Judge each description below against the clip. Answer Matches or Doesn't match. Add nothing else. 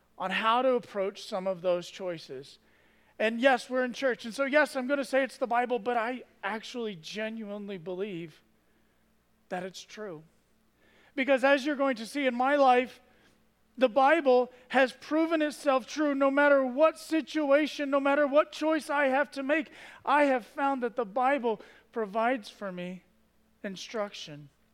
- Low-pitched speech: Doesn't match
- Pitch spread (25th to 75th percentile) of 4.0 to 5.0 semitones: Matches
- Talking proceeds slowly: Doesn't match